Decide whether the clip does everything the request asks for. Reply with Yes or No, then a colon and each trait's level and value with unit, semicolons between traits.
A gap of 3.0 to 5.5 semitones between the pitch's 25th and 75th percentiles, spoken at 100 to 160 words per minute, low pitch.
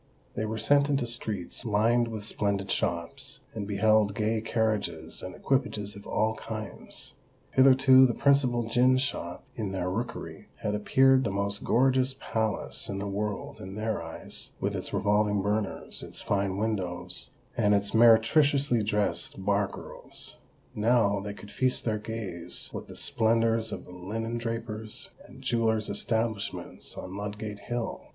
No: narrow, 2.6 semitones; average, 145 wpm; low, 110 Hz